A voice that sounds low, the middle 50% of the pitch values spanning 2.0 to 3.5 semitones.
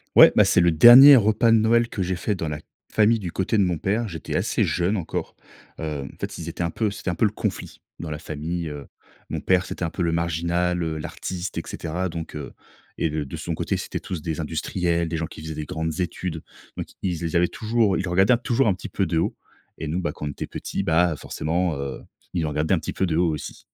Yes: very low, 85 Hz; average, 3.1 semitones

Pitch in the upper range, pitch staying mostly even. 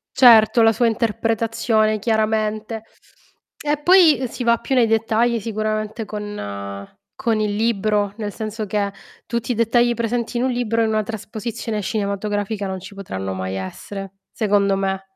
Yes: high, 215 Hz; narrow, 2.2 semitones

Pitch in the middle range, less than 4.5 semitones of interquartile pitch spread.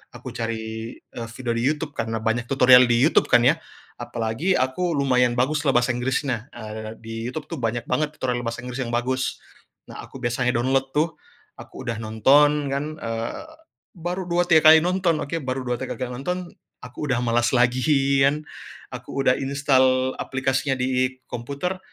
No: low, 130 Hz; average, 3.5 semitones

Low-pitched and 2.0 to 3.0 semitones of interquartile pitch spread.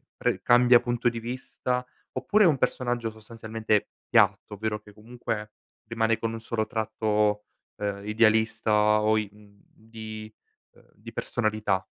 No: low, 110 Hz; narrow, 1.6 semitones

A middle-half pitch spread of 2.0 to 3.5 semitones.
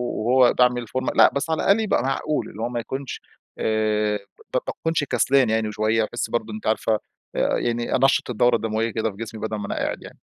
Yes: average, 2.9 semitones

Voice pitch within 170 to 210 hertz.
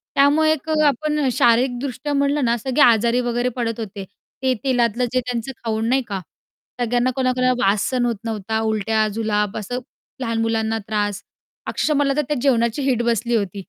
No: high, 240 Hz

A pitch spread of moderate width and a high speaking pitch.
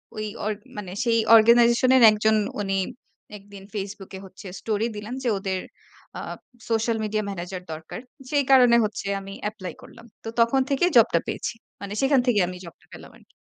Yes: average, 3.2 semitones; high, 215 Hz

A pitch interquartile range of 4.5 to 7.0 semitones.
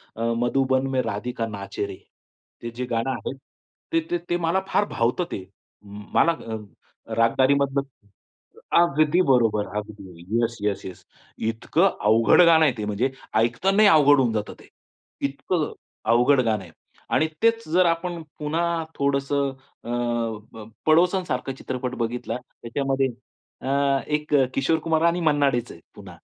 Yes: wide, 5.4 semitones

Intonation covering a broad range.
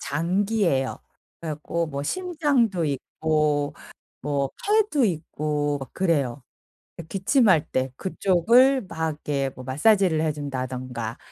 Yes: wide, 5.7 semitones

